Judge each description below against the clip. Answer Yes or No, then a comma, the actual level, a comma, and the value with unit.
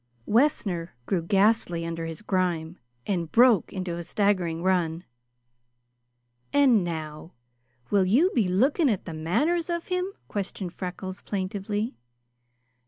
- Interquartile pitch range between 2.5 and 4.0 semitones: No, average, 4.9 semitones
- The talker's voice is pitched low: No, high, 190 Hz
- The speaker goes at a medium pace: No, slow, 120 wpm